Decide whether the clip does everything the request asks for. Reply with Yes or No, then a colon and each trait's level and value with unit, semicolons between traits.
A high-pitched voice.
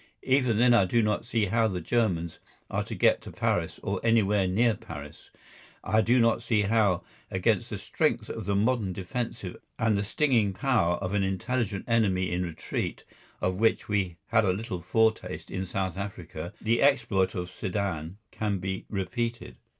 No: low, 100 Hz